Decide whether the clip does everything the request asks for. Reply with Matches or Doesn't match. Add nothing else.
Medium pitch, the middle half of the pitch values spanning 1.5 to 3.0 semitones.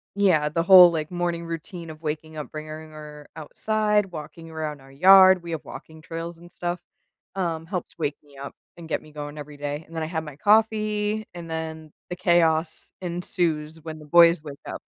Matches